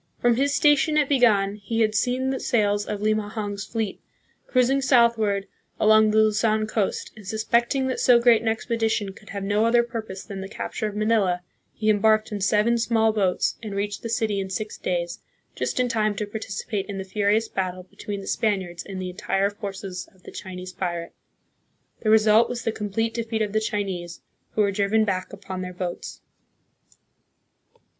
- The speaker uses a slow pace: No, average, 180 wpm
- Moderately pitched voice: No, high, 215 Hz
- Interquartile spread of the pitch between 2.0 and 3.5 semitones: Yes, narrow, 2.4 semitones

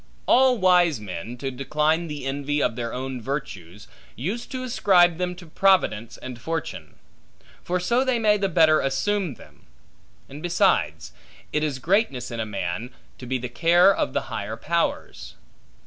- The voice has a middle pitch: Yes, medium, 150 Hz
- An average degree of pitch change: No, wide, 6.7 semitones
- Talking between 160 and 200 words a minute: Yes, average, 165 wpm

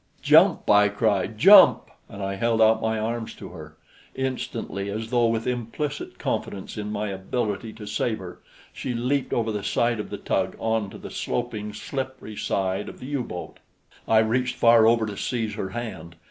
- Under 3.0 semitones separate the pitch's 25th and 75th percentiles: Yes, narrow, 2.5 semitones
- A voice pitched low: Yes, low, 110 Hz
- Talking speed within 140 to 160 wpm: No, average, 180 wpm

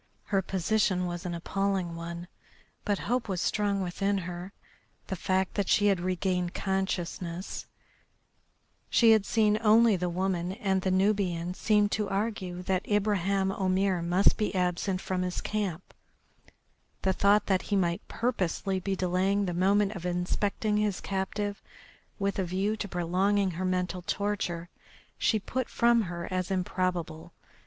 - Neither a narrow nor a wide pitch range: No, narrow, 2.3 semitones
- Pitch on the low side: No, high, 190 Hz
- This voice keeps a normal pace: Yes, average, 150 wpm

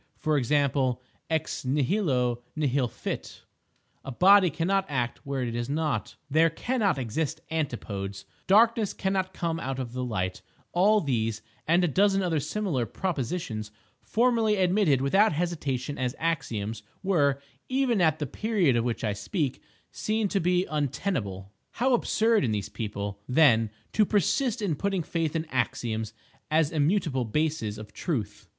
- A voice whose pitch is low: No, medium, 150 Hz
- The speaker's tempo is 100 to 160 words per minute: Yes, average, 140 wpm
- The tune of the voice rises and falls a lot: Yes, wide, 7.4 semitones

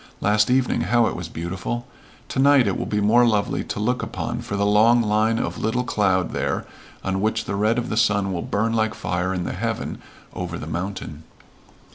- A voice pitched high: No, low, 105 Hz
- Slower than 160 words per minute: No, fast, 205 wpm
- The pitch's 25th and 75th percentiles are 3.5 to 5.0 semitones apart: No, average, 3.1 semitones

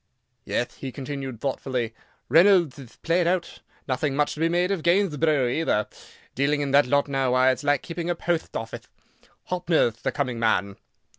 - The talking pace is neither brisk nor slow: Yes, average, 170 wpm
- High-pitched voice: No, medium, 145 Hz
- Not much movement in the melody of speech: No, average, 4.5 semitones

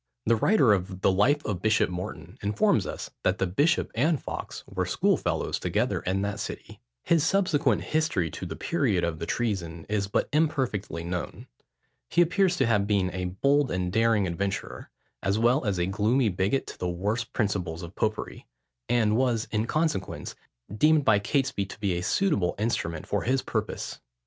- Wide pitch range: Yes, wide, 6.1 semitones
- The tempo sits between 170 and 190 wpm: Yes, average, 175 wpm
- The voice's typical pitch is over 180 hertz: No, low, 105 Hz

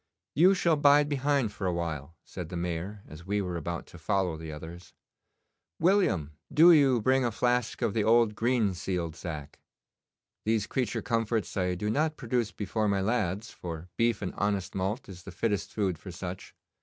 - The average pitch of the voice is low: Yes, low, 100 Hz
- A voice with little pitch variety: No, wide, 5.4 semitones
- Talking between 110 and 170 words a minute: No, average, 180 wpm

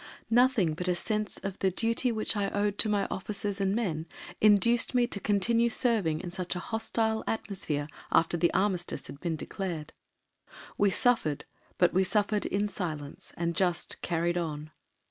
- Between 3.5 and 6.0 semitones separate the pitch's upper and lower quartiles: Yes, average, 3.9 semitones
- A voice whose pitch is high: Yes, high, 195 Hz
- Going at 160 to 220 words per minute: Yes, average, 165 wpm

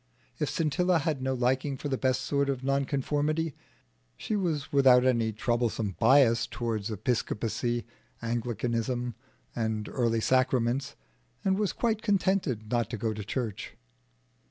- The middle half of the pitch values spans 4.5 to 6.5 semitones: No, average, 3.5 semitones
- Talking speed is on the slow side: Yes, slow, 130 wpm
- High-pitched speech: No, low, 125 Hz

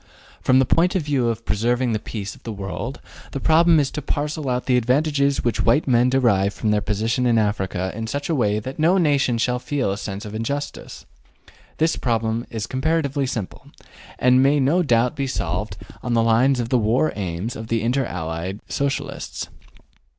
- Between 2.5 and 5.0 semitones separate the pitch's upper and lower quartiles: Yes, average, 4.4 semitones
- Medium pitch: No, low, 125 Hz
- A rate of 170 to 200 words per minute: Yes, average, 195 wpm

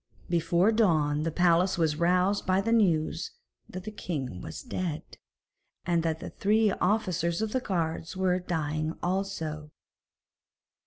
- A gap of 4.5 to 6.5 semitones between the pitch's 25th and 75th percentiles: No, average, 3.4 semitones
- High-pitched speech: No, medium, 175 Hz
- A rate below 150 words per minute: Yes, average, 140 wpm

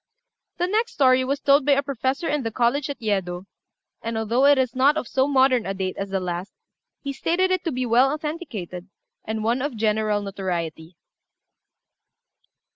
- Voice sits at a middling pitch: No, very high, 255 Hz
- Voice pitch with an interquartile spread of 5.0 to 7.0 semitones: Yes, wide, 5.6 semitones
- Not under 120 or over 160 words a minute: No, average, 180 wpm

